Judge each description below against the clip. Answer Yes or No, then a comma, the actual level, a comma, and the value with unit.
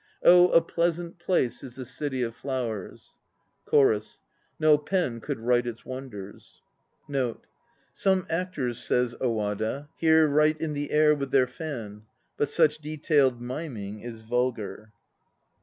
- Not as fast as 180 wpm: Yes, average, 140 wpm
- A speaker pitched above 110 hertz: Yes, low, 135 Hz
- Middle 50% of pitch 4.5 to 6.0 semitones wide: Yes, average, 4.8 semitones